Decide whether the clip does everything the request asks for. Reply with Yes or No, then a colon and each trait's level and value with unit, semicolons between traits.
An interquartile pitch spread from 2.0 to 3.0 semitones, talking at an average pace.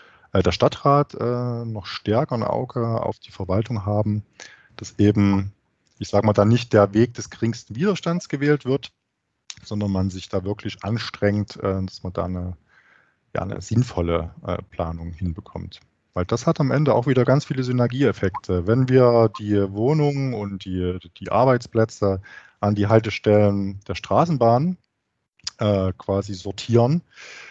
No: average, 3.9 semitones; average, 150 wpm